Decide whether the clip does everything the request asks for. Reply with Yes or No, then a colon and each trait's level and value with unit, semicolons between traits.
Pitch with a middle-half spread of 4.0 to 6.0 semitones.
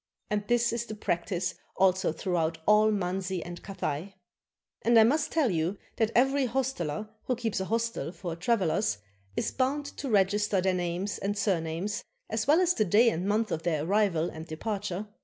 Yes: average, 4.6 semitones